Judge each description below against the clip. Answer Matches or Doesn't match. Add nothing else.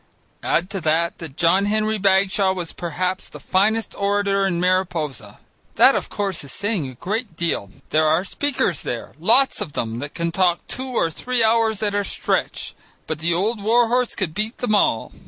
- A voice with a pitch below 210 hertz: Matches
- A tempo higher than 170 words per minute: Matches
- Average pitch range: Matches